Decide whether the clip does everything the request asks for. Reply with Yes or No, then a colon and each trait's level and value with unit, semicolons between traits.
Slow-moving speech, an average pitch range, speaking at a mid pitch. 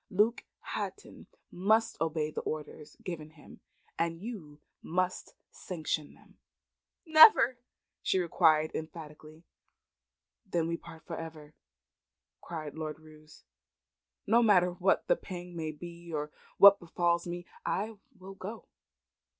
Yes: slow, 120 wpm; average, 3.5 semitones; medium, 170 Hz